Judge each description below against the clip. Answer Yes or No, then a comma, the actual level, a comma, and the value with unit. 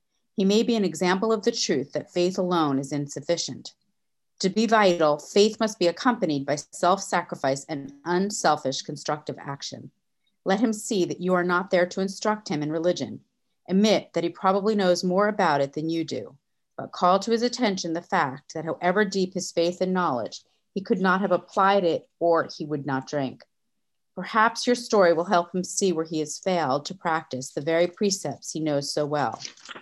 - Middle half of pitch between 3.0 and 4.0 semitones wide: No, average, 4.4 semitones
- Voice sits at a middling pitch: Yes, medium, 180 Hz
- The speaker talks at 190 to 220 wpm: Yes, average, 195 wpm